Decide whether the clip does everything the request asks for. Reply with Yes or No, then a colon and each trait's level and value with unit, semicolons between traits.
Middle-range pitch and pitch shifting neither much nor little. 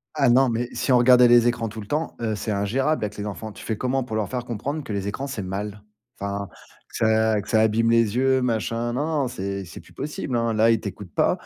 No: low, 115 Hz; average, 3.2 semitones